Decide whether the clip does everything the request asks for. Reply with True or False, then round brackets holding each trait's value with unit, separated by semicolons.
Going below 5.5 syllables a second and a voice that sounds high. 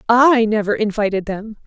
True (4.9 syllables/s; 225 Hz)